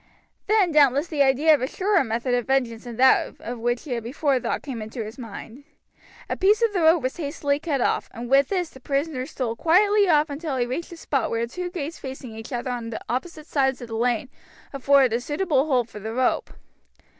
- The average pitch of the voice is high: Yes, very high, 270 Hz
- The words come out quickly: Yes, fast, 220 wpm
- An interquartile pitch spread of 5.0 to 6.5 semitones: No, average, 4.6 semitones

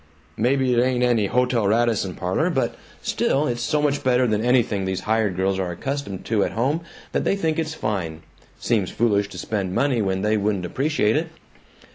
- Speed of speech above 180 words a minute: Yes, average, 190 wpm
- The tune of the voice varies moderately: Yes, average, 4.6 semitones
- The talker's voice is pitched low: Yes, low, 115 Hz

